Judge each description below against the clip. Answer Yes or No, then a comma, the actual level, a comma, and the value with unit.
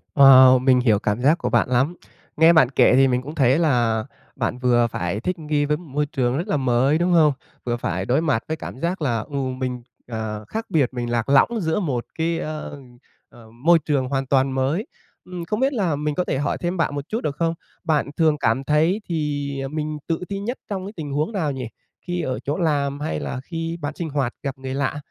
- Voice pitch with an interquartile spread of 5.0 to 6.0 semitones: No, average, 4.2 semitones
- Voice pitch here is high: No, medium, 145 Hz